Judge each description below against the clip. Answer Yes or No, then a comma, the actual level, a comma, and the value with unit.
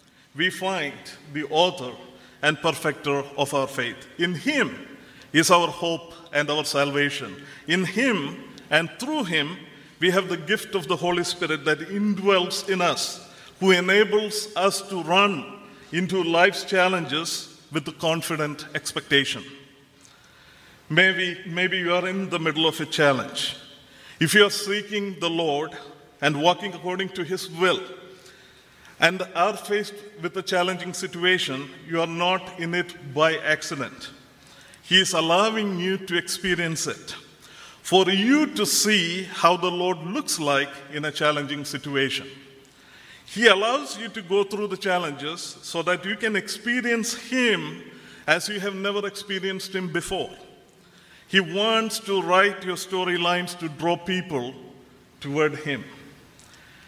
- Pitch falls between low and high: Yes, medium, 175 Hz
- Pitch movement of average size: Yes, average, 4.0 semitones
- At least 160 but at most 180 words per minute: No, average, 140 wpm